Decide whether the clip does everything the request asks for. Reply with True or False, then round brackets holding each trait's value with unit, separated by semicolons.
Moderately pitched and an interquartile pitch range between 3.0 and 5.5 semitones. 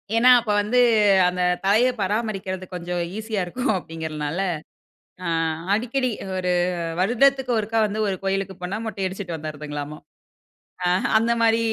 False (195 Hz; 4.1 semitones)